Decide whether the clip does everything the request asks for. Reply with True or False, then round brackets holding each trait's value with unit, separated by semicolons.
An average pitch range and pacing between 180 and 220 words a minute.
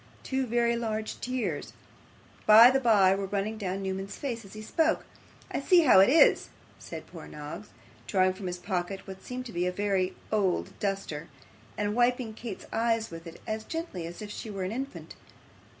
True (3.9 semitones; 185 wpm)